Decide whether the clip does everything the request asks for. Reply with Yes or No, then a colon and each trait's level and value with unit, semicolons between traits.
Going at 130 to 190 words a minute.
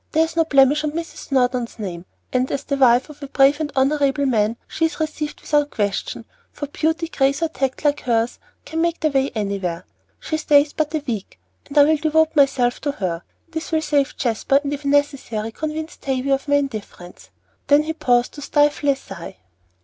No: fast, 205 wpm